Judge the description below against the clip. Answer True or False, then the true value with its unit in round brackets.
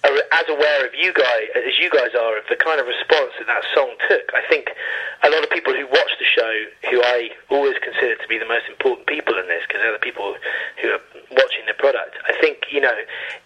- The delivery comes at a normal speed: False (240 wpm)